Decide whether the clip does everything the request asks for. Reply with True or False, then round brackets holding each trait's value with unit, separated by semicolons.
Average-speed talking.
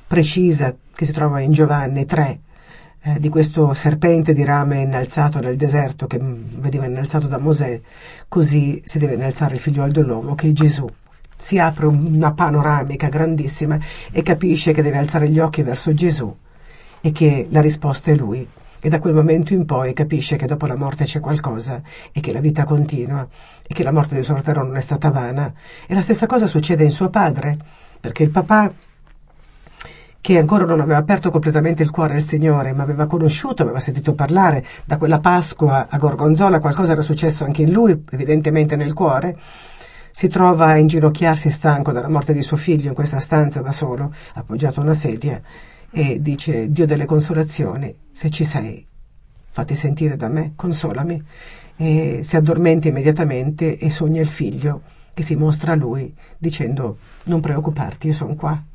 False (175 wpm)